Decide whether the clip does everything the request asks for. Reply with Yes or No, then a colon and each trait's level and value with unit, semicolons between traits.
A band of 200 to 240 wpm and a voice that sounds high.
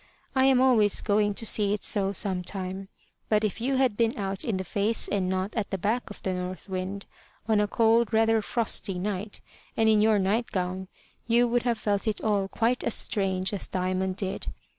Yes: fast, 205 wpm; high, 205 Hz